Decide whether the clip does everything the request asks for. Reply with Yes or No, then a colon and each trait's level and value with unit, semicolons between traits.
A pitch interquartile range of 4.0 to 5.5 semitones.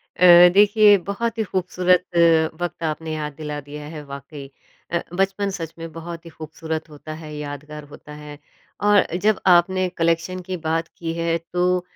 No: average, 3.0 semitones